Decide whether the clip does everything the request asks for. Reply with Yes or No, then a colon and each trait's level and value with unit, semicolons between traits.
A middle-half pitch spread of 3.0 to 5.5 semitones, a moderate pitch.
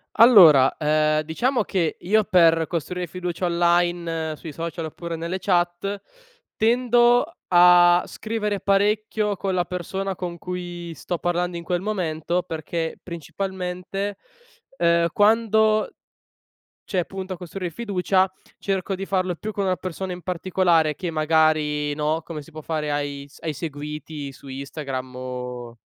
Yes: average, 3.4 semitones; medium, 175 Hz